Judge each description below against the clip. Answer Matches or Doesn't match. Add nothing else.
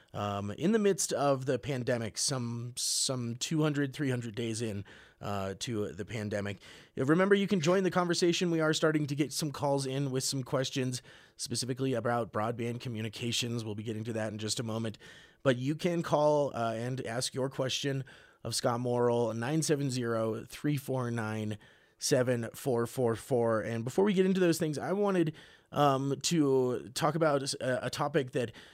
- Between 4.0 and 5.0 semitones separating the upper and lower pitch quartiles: Matches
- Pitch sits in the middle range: Doesn't match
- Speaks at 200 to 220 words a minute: Doesn't match